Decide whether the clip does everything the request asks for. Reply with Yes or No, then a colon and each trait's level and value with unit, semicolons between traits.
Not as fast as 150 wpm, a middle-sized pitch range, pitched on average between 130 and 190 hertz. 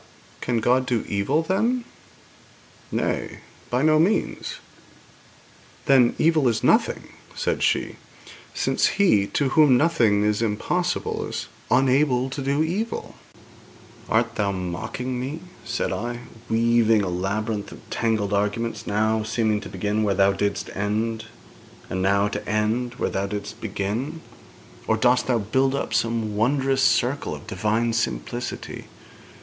No: slow, 135 wpm; average, 4.2 semitones; low, 115 Hz